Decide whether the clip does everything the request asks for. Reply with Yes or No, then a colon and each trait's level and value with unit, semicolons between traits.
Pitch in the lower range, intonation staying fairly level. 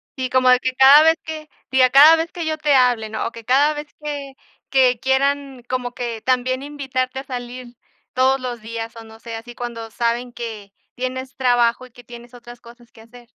No: very high, 255 Hz; narrow, 2.1 semitones